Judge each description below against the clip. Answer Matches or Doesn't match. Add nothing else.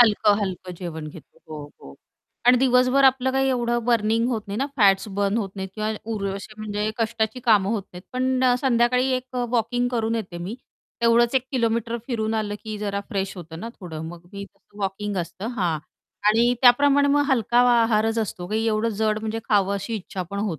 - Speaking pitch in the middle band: Doesn't match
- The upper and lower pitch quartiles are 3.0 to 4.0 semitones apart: Matches